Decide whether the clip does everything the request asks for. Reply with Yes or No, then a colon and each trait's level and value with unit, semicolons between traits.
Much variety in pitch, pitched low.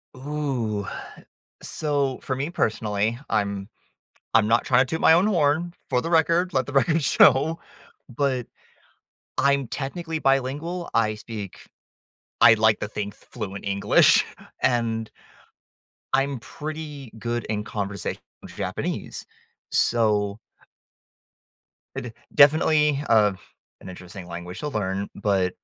Yes: wide, 5.7 semitones; low, 125 Hz